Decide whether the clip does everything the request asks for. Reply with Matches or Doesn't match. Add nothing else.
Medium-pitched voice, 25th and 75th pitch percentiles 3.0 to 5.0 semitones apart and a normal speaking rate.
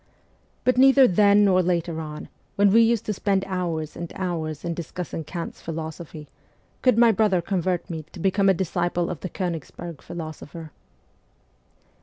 Matches